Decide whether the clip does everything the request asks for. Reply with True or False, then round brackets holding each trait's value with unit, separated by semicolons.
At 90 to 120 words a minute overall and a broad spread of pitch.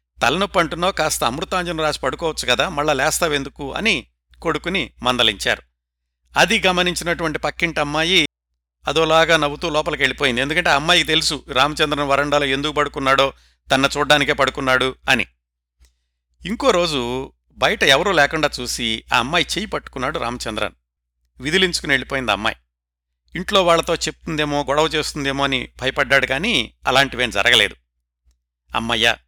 True (115 wpm; 7.8 semitones)